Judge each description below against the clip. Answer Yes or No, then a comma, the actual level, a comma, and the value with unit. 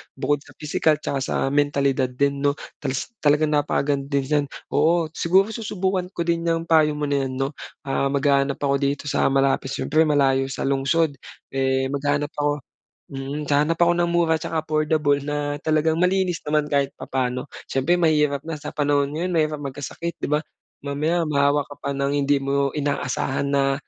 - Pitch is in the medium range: Yes, medium, 145 Hz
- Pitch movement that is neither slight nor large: No, narrow, 2.1 semitones